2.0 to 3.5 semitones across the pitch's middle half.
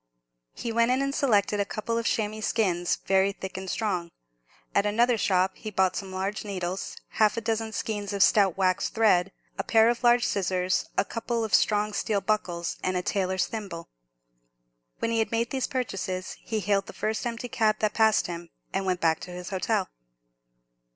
Yes: average, 3.1 semitones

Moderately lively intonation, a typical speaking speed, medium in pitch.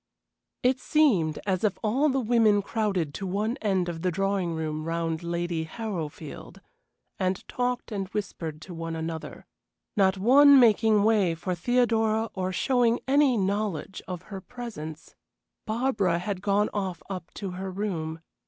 No: average, 4.6 semitones; average, 150 wpm; high, 195 Hz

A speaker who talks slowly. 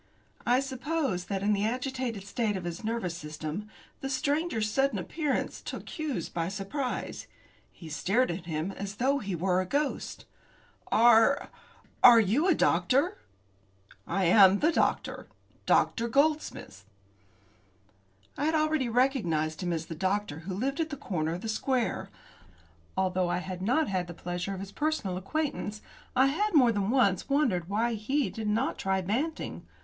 No: average, 155 wpm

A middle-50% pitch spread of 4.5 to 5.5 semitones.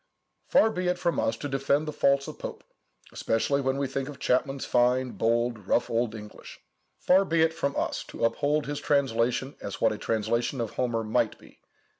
No: average, 3.6 semitones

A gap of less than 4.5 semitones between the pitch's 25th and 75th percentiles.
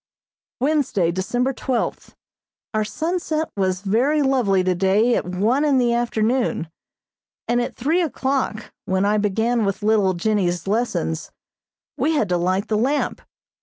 No: wide, 5.4 semitones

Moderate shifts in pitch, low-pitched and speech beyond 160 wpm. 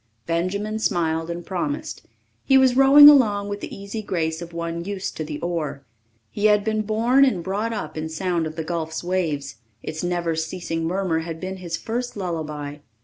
No: average, 4.4 semitones; medium, 175 Hz; average, 185 wpm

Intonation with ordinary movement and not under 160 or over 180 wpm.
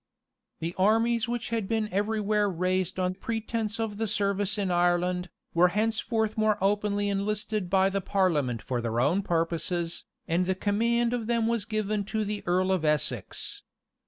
Yes: average, 3.2 semitones; average, 165 wpm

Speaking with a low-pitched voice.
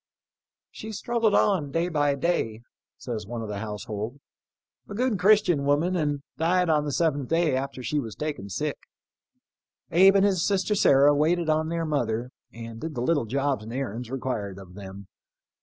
No: medium, 145 Hz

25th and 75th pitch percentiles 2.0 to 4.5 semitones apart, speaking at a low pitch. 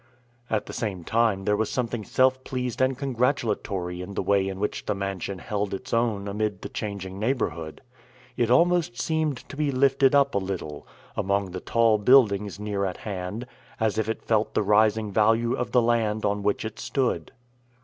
Yes: average, 3.8 semitones; low, 110 Hz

